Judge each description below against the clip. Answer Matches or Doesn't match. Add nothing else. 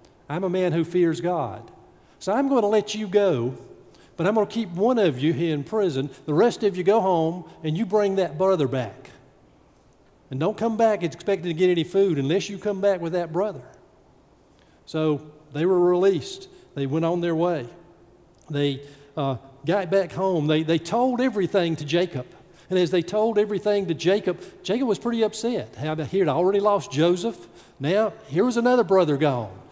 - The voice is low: Doesn't match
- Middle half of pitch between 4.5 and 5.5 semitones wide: Matches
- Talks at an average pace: Matches